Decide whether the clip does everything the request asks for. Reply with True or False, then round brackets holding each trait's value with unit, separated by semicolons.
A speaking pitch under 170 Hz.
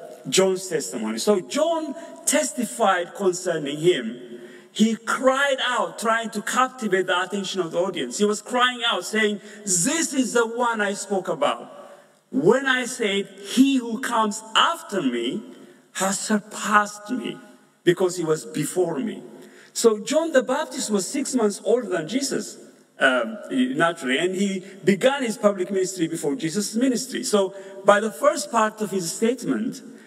False (210 Hz)